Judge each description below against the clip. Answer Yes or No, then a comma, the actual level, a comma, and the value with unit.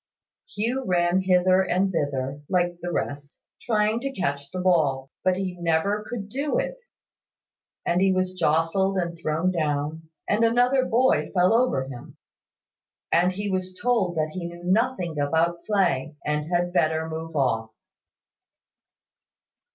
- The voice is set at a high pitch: No, medium, 180 Hz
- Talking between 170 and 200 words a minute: No, average, 145 wpm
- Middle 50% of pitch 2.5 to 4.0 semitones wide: Yes, average, 3.7 semitones